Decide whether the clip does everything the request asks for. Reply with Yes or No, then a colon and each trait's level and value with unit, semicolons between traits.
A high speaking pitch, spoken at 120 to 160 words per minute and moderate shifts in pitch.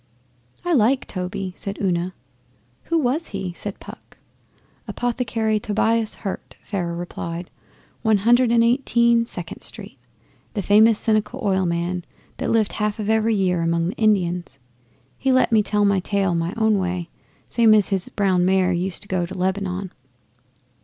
Yes: high, 200 Hz; average, 155 wpm; average, 3.5 semitones